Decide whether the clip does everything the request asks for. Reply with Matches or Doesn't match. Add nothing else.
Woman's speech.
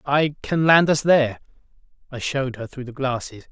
Doesn't match